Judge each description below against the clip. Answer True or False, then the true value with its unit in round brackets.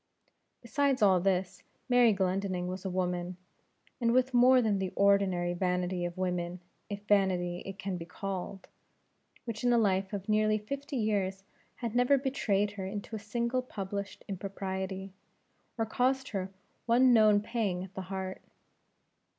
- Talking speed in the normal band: True (150 wpm)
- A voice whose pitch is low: False (200 Hz)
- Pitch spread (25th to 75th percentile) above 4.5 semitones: False (3.6 semitones)